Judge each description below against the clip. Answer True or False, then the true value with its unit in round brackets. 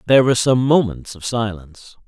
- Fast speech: False (175 wpm)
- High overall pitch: False (115 Hz)